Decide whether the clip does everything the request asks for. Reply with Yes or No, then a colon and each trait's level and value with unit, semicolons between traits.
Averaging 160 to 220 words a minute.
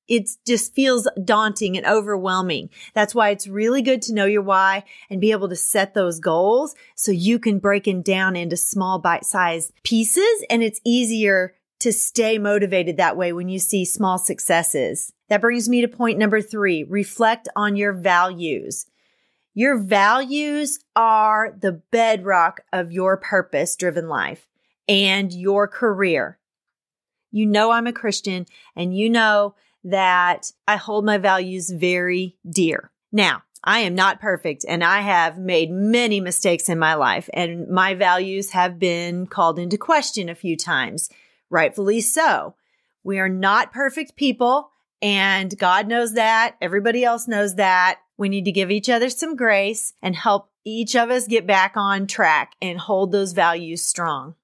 Yes: average, 165 wpm